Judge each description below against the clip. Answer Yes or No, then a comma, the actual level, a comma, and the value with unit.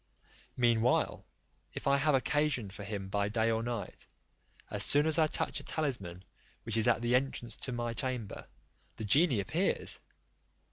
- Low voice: Yes, low, 120 Hz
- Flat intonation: No, average, 4.0 semitones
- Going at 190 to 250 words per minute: No, average, 160 wpm